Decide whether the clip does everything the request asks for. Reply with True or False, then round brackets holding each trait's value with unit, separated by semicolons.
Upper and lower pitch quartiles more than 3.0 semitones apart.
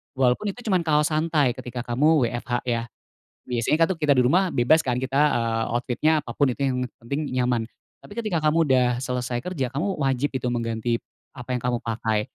True (4.0 semitones)